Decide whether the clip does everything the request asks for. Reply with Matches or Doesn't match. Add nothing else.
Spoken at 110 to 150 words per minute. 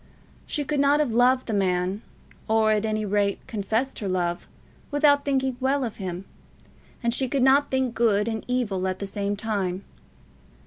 Doesn't match